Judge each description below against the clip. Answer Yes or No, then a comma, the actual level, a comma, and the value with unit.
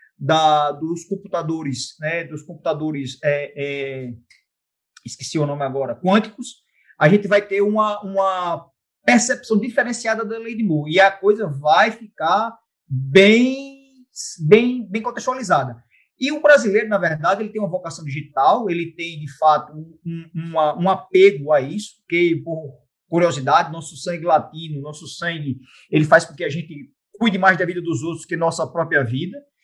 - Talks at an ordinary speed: Yes, average, 160 wpm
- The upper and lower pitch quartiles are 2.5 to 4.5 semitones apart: No, wide, 5.4 semitones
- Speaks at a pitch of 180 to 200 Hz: No, medium, 170 Hz